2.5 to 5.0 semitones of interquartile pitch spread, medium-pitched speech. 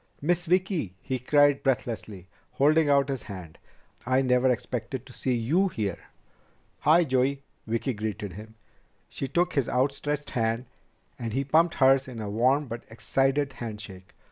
No: average, 4.2 semitones; low, 130 Hz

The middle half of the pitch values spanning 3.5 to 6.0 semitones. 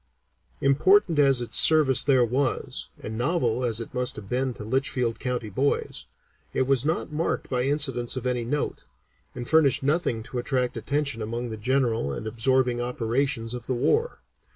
No: average, 2.7 semitones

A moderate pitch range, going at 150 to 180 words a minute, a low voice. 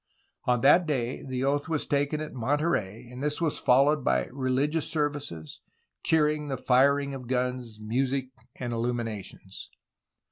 No: average, 3.2 semitones; average, 140 wpm; low, 130 Hz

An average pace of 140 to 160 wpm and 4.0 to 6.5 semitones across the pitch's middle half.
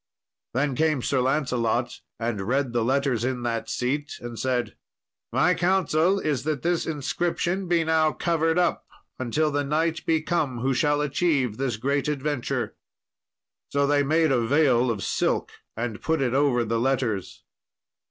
Yes: average, 155 wpm; average, 4.3 semitones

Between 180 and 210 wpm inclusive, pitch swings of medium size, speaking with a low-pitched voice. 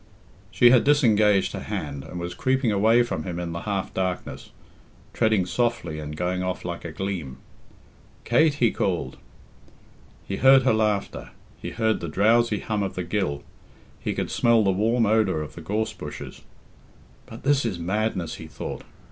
No: average, 170 wpm; average, 4.4 semitones; low, 100 Hz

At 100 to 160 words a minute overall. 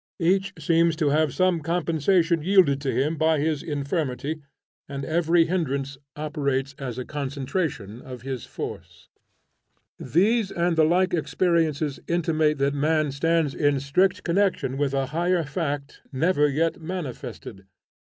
Yes: slow, 135 wpm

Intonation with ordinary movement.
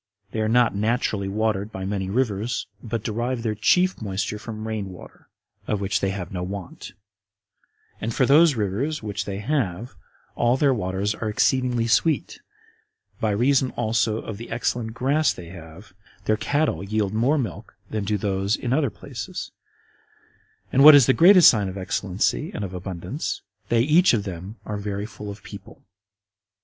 Yes: average, 3.7 semitones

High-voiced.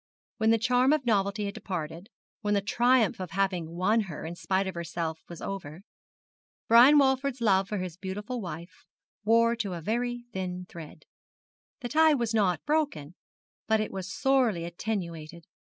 Yes: high, 200 Hz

